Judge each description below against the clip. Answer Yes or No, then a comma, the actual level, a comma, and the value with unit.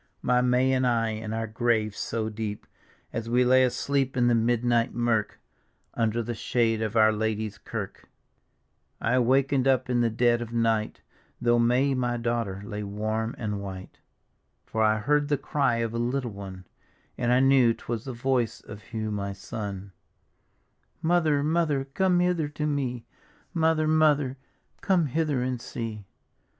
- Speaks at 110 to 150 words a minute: No, average, 160 wpm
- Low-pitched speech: Yes, low, 120 Hz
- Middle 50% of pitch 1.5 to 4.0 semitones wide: Yes, average, 3.4 semitones